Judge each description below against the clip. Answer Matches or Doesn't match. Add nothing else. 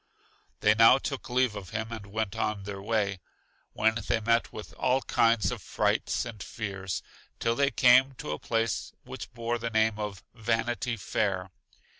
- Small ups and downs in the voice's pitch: Matches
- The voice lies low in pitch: Matches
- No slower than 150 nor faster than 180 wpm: Matches